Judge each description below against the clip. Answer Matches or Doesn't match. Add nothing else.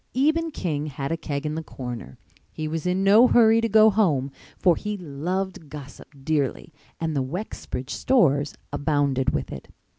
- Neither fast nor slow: Matches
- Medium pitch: Matches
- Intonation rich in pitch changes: Matches